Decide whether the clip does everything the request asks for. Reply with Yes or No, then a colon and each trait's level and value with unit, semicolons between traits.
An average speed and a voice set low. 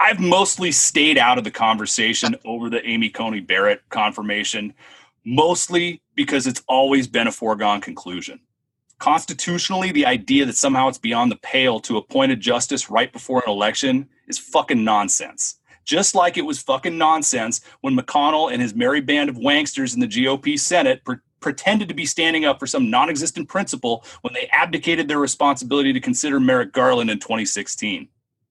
No: average, 170 wpm; medium, 150 Hz